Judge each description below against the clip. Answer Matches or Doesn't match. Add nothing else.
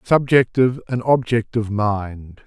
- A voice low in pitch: Matches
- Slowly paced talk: Matches